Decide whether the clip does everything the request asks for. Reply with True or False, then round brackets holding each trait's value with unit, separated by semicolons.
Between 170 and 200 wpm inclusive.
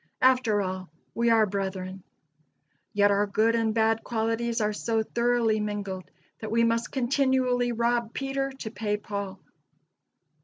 False (140 wpm)